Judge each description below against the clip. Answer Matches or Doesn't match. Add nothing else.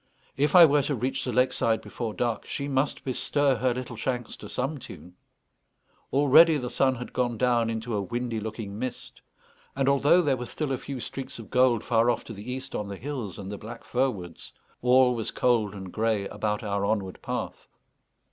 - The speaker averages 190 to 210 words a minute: Matches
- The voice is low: Matches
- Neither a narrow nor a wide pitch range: Matches